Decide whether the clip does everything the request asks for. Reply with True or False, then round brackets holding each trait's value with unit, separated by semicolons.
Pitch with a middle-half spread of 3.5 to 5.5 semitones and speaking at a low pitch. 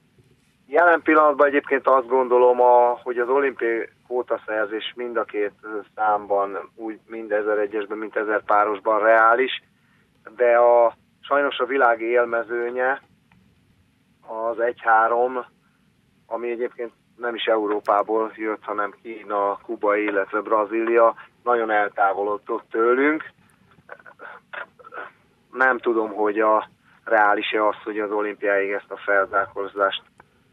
False (2.8 semitones; 115 Hz)